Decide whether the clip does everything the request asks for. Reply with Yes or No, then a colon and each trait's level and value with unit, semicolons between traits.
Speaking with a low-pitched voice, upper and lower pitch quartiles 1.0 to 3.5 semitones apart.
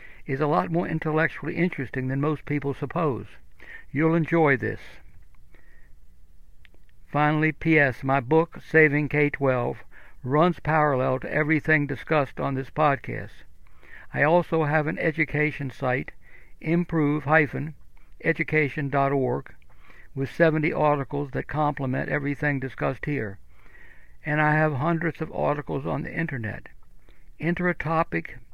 No: medium, 150 Hz; average, 3.0 semitones